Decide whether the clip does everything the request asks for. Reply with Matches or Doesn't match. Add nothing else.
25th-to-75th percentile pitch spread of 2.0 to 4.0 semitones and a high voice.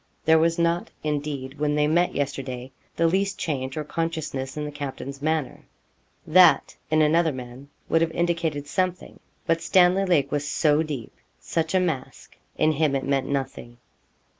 Doesn't match